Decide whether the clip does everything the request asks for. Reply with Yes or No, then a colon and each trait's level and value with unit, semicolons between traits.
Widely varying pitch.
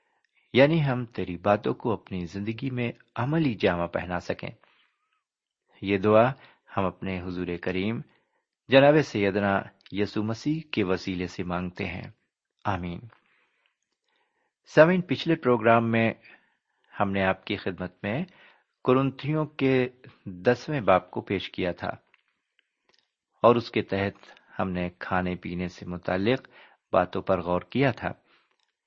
Yes: wide, 6.2 semitones